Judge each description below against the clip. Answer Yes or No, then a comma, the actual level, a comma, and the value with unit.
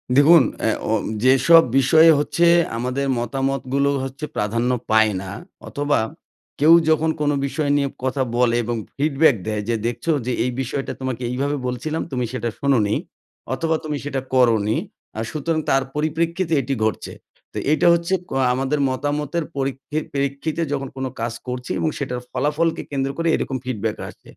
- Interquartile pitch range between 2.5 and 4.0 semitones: Yes, average, 3.2 semitones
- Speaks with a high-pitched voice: No, low, 135 Hz